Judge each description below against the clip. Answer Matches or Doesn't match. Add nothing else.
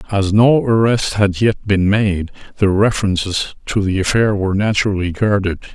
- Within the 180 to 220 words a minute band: Doesn't match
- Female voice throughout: Doesn't match